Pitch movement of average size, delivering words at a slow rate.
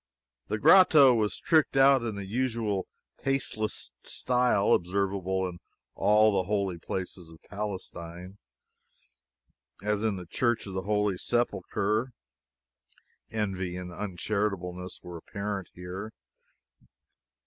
Yes: average, 3.1 semitones; slow, 110 wpm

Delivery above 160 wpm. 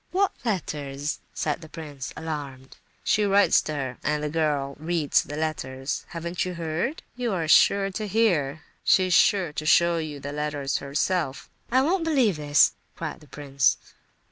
No: average, 155 wpm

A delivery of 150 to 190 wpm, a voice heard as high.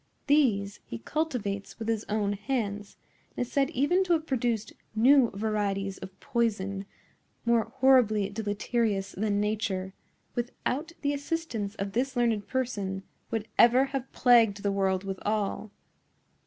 No: slow, 135 wpm; high, 220 Hz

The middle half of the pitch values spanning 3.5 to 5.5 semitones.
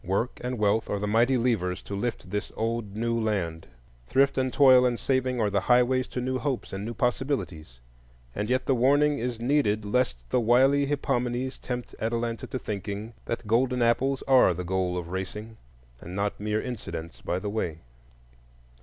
Yes: average, 4.0 semitones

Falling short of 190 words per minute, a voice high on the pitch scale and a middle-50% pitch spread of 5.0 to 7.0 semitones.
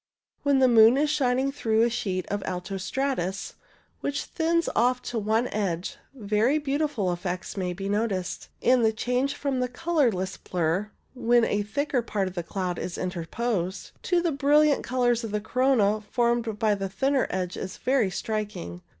Yes: average, 175 wpm; high, 225 Hz; wide, 5.5 semitones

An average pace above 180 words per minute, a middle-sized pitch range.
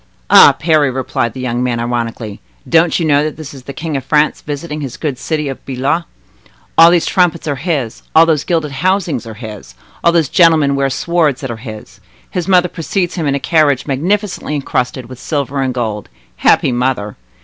Yes: average, 195 wpm; average, 4.5 semitones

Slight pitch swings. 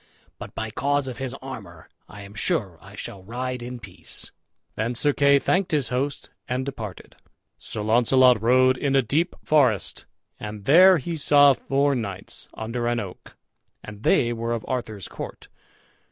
No: average, 4.1 semitones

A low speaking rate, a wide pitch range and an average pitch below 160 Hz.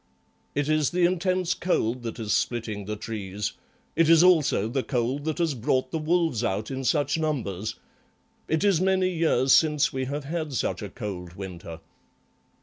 No: average, 170 wpm; wide, 6.8 semitones; low, 135 Hz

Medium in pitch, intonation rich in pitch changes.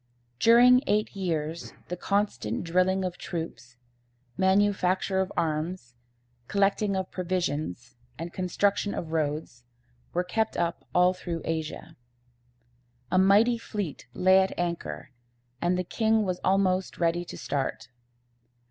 No: medium, 180 Hz; average, 3.2 semitones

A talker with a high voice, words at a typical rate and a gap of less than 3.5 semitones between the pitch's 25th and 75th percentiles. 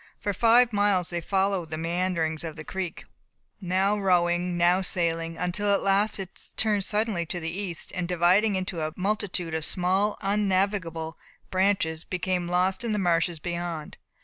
No: medium, 180 Hz; average, 160 wpm; average, 2.7 semitones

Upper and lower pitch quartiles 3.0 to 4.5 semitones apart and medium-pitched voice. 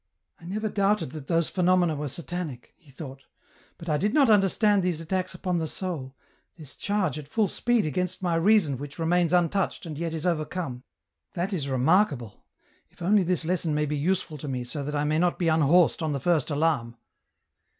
Yes: average, 3.6 semitones; medium, 165 Hz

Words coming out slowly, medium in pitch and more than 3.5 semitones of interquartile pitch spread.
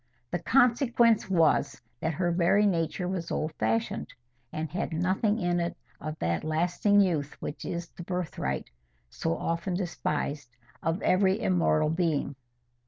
Yes: slow, 130 wpm; medium, 170 Hz; average, 4.0 semitones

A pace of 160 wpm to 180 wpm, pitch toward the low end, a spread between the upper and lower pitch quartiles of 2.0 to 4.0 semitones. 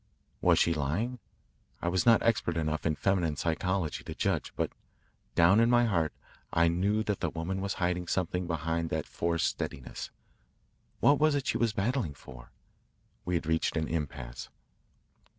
Yes: average, 165 wpm; very low, 85 Hz; average, 3.7 semitones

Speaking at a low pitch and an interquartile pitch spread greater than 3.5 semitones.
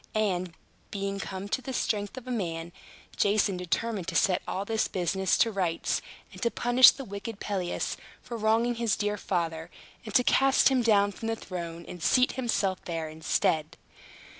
No: high, 200 Hz; average, 4.3 semitones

